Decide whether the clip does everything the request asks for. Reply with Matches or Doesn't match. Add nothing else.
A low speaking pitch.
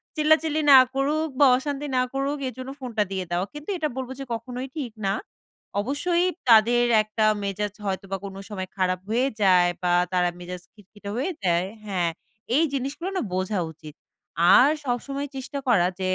Doesn't match